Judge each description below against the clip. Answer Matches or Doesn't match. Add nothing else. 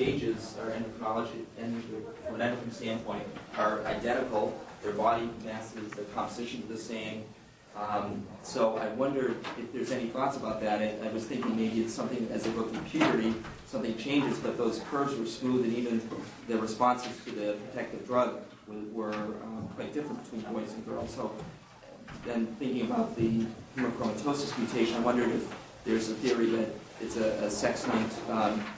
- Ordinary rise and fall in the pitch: Doesn't match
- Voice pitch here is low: Matches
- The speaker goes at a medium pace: Matches